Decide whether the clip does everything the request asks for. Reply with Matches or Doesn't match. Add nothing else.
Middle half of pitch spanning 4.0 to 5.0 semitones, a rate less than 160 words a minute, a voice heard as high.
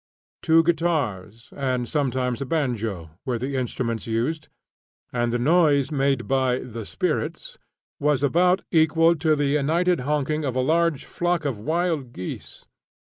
Doesn't match